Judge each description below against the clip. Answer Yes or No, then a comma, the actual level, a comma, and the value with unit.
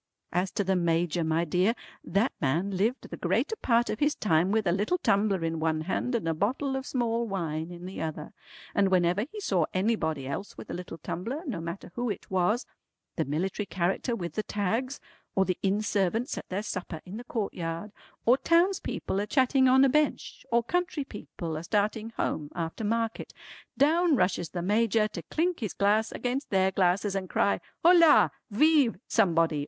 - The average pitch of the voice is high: Yes, high, 200 Hz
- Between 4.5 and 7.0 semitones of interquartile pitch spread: Yes, wide, 5.4 semitones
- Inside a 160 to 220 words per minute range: Yes, average, 190 wpm